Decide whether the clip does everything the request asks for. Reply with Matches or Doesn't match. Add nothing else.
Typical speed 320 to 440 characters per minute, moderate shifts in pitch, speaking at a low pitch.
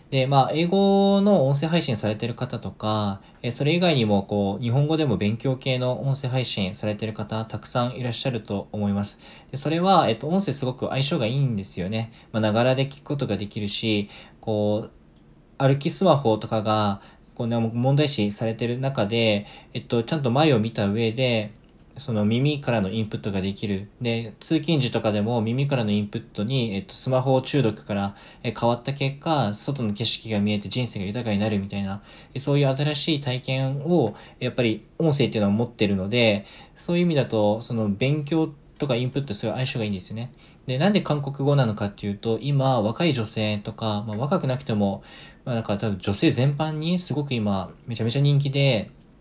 Matches